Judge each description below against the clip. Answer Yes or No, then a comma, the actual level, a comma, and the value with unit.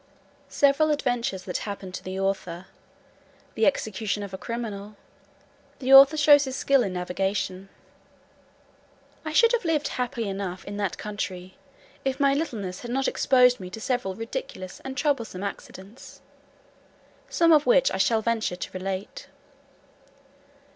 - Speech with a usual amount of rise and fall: No, wide, 6.2 semitones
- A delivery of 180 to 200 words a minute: No, average, 140 wpm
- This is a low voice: No, high, 225 Hz